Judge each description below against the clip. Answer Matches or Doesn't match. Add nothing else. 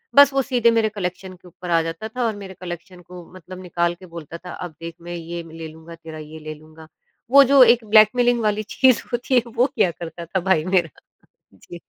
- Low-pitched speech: Doesn't match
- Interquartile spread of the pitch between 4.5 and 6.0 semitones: Matches